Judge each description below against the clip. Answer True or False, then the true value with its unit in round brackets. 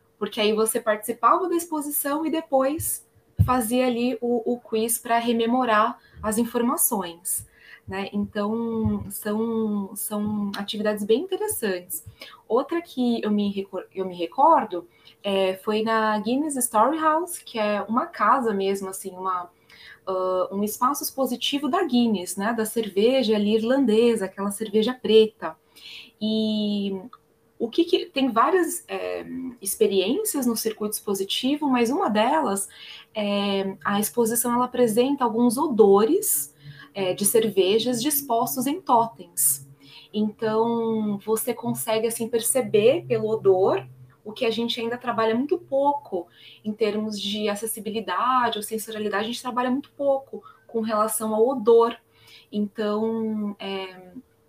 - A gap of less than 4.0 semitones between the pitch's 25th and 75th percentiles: True (3.2 semitones)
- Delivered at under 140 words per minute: True (130 wpm)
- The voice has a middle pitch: False (220 Hz)